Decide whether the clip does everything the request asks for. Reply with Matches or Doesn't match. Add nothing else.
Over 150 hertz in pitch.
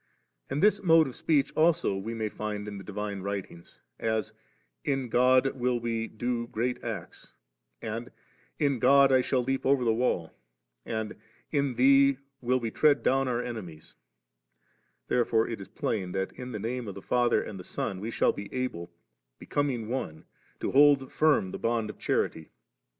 Doesn't match